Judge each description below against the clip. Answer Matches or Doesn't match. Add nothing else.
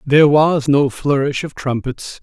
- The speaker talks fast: Doesn't match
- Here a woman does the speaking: Doesn't match